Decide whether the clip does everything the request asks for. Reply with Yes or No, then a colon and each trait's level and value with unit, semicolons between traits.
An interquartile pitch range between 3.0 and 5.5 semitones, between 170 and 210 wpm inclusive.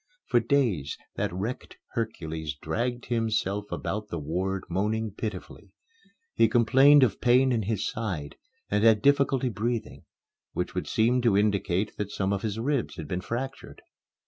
No: average, 3.9 semitones; average, 155 wpm